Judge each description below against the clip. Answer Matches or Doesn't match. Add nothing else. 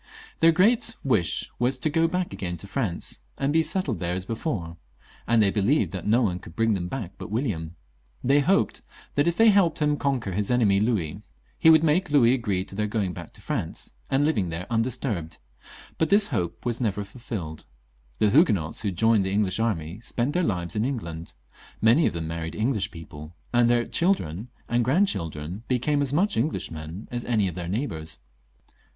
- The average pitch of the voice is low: Matches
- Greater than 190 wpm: Matches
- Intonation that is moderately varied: Doesn't match